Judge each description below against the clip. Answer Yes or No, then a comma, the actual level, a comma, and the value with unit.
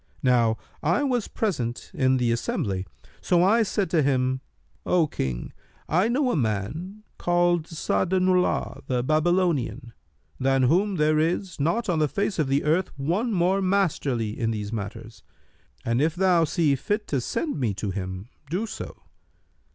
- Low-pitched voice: No, medium, 155 Hz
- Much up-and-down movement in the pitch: Yes, wide, 6.9 semitones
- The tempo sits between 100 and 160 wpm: Yes, average, 155 wpm